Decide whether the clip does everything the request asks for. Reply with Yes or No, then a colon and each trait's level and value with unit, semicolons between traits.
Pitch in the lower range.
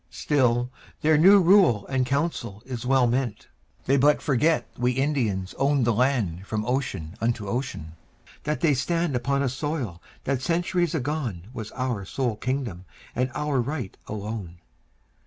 Yes: low, 130 Hz